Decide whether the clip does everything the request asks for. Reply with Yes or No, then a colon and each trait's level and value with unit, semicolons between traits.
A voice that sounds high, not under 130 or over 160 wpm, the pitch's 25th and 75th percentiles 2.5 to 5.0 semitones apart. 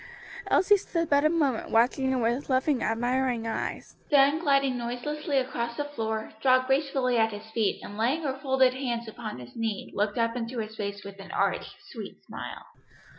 No: very high, 250 Hz; average, 180 wpm; average, 3.5 semitones